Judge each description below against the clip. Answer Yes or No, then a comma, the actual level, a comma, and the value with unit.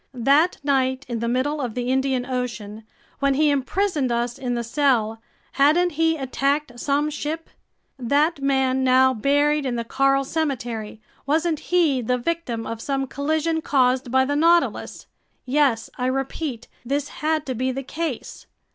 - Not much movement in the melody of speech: No, average, 3.1 semitones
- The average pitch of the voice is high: Yes, very high, 270 Hz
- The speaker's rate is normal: Yes, average, 155 wpm